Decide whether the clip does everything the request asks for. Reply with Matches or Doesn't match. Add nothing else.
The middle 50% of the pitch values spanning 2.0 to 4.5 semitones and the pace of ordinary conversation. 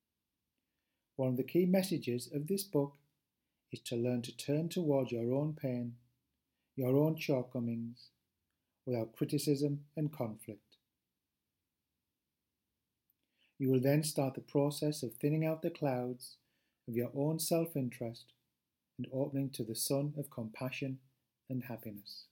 Doesn't match